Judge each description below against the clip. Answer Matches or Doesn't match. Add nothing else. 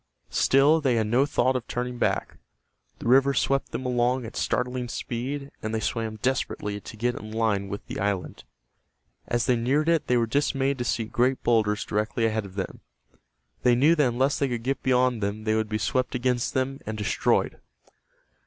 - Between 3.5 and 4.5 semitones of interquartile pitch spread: Doesn't match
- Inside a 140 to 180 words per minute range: Doesn't match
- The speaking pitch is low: Matches